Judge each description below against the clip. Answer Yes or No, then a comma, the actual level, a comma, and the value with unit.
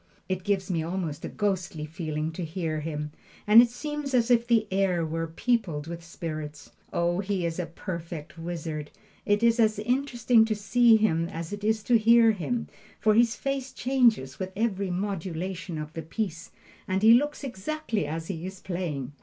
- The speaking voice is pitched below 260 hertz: Yes, high, 190 Hz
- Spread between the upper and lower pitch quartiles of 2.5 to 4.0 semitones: No, wide, 5.6 semitones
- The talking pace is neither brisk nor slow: Yes, average, 180 wpm